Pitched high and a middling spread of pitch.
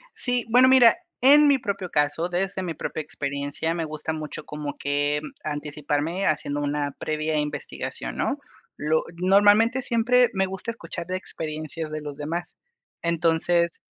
No: medium, 165 Hz; average, 4.7 semitones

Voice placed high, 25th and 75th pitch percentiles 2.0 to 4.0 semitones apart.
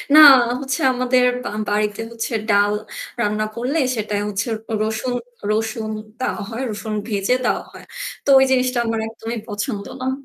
Yes: high, 225 Hz; average, 3.1 semitones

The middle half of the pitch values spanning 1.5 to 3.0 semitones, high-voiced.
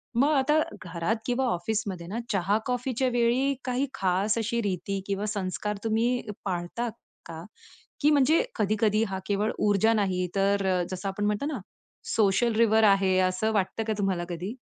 No: average, 3.6 semitones; high, 210 Hz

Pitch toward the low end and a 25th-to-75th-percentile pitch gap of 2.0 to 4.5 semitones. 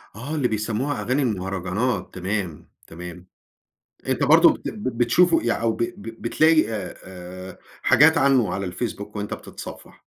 No: low, 110 Hz; average, 5.3 semitones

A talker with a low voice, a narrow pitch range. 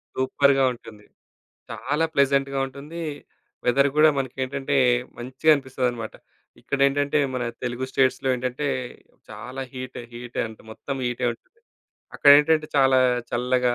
Yes: low, 130 Hz; narrow, 2.1 semitones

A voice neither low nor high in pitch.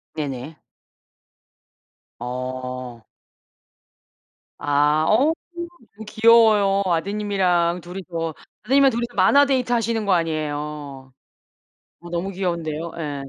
Yes: medium, 170 Hz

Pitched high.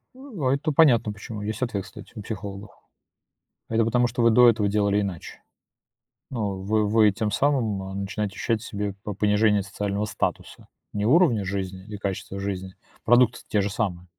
No: low, 105 Hz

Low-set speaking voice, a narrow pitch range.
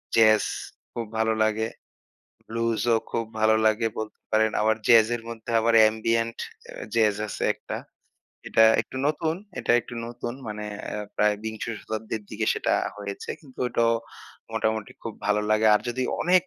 Yes: low, 110 Hz; narrow, 1.2 semitones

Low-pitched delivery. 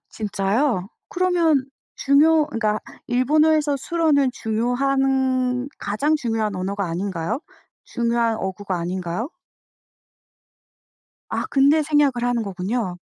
No: high, 245 Hz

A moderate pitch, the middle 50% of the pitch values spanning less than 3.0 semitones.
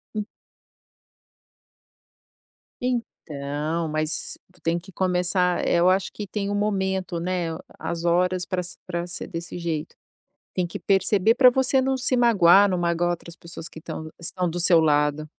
Yes: medium, 180 Hz; narrow, 2.6 semitones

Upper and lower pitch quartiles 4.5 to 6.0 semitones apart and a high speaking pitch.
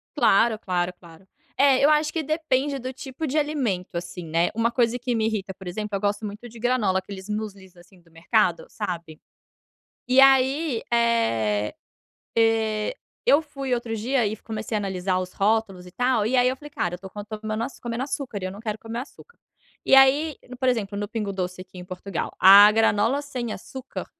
Yes: average, 5.2 semitones; high, 220 Hz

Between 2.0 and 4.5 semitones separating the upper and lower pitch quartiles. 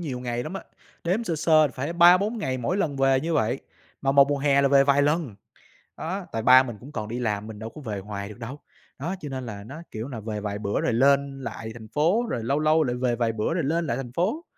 No: average, 5.3 semitones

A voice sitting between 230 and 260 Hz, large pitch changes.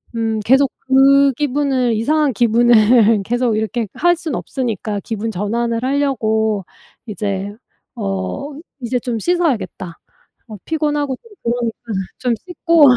No: high, 240 Hz; average, 4.2 semitones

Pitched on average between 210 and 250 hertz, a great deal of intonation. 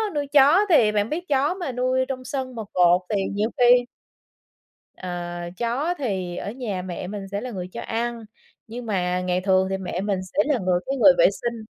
Yes: high, 225 Hz; wide, 5.7 semitones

